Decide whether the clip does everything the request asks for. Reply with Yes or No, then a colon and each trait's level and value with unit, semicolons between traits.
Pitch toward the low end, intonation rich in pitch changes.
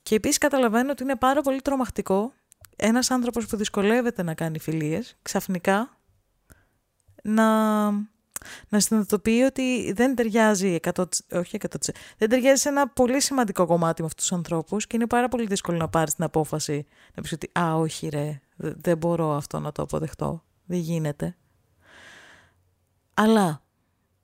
No: high, 190 Hz; wide, 6.8 semitones